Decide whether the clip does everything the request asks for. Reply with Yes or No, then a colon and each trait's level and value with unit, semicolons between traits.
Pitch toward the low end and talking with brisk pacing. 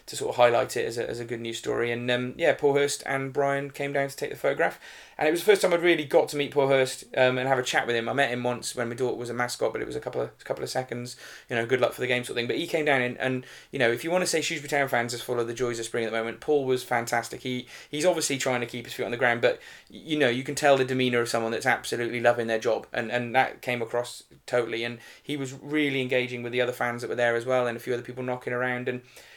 Yes: low, 125 Hz; fast, 325 wpm